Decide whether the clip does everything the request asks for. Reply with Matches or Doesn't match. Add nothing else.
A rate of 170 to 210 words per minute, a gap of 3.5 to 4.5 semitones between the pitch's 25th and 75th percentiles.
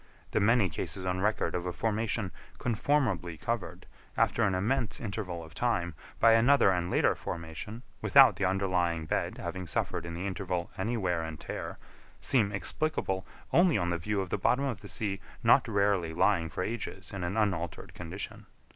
Matches